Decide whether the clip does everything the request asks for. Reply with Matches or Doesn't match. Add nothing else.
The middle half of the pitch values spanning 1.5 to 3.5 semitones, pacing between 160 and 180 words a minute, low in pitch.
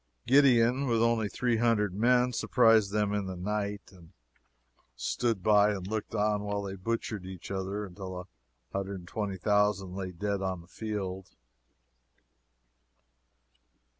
Doesn't match